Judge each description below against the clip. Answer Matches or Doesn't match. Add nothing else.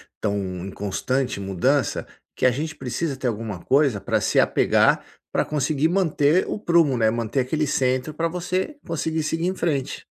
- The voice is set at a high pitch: Doesn't match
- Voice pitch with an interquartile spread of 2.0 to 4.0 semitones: Doesn't match